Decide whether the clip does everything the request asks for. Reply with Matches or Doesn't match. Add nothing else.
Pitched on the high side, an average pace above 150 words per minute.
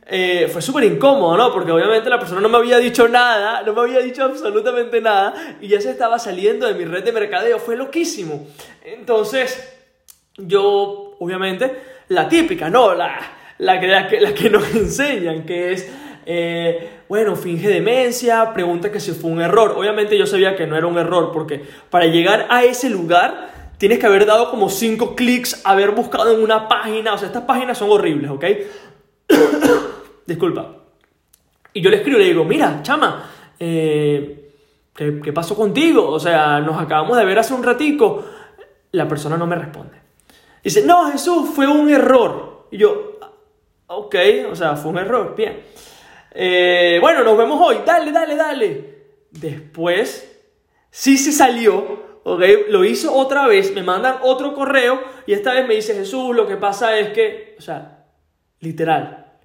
Matches